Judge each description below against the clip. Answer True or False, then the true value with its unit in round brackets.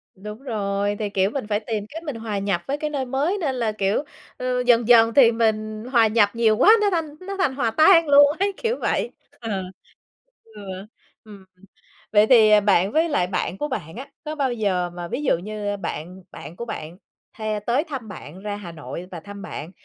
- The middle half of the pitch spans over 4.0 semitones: True (5.1 semitones)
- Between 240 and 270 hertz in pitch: False (220 Hz)